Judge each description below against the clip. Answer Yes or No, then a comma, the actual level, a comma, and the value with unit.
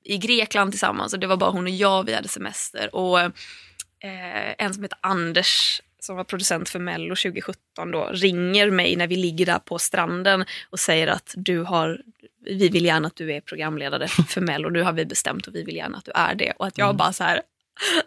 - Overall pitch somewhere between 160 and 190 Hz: Yes, medium, 185 Hz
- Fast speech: Yes, fast, 220 wpm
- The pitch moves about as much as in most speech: No, narrow, 2.0 semitones